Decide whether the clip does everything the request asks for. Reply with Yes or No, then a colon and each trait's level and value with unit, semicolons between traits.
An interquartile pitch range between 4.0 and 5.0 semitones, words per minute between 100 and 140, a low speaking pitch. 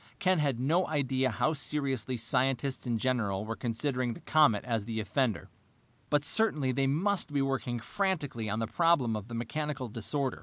No: average, 4.3 semitones; average, 175 wpm; low, 130 Hz